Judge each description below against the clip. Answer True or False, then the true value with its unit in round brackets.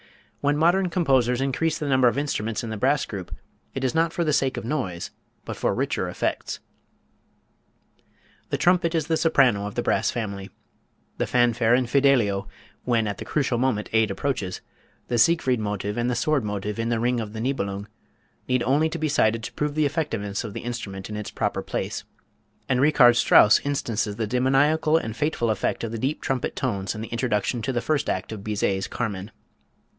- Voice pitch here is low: True (120 Hz)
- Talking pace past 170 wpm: True (190 wpm)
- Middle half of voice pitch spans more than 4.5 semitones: True (5.0 semitones)